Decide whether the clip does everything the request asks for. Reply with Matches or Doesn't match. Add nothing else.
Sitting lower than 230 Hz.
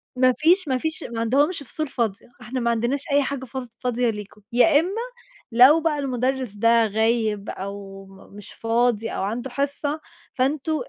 Doesn't match